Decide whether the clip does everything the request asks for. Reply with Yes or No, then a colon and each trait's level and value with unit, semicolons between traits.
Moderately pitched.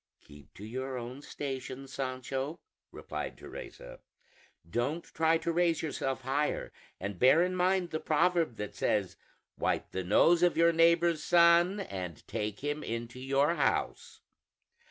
Yes: medium, 145 Hz